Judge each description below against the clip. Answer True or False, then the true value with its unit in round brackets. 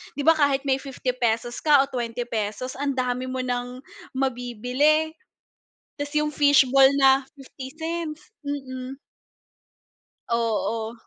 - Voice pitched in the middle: False (265 Hz)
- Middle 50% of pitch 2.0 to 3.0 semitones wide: True (2.6 semitones)